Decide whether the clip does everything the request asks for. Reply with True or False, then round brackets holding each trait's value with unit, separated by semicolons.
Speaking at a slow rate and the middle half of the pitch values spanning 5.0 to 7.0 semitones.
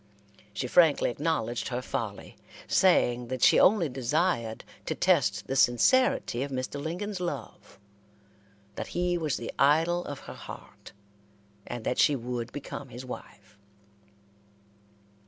True (130 wpm; 5.5 semitones)